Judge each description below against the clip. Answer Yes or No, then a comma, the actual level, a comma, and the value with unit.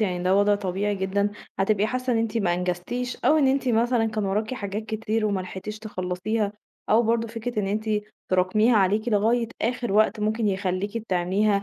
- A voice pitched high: Yes, high, 215 Hz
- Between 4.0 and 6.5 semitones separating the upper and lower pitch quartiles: No, average, 2.7 semitones